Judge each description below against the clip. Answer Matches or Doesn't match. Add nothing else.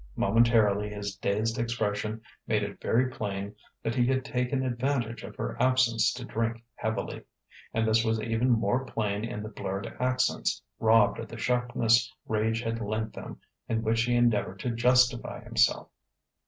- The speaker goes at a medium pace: Matches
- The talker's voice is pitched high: Doesn't match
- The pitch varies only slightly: Matches